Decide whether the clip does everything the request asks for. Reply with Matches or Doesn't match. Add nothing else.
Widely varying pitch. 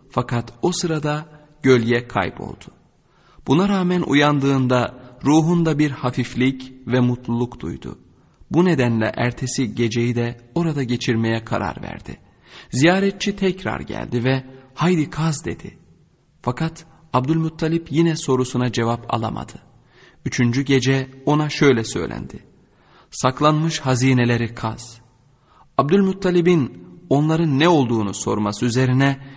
Doesn't match